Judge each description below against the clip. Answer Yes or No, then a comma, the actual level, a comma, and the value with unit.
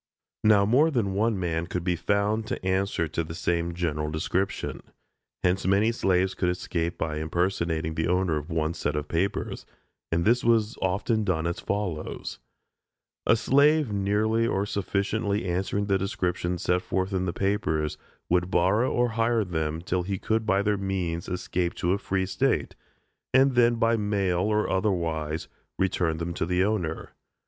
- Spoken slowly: No, average, 165 wpm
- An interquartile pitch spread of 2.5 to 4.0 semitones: Yes, average, 3.4 semitones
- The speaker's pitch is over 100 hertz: No, very low, 95 Hz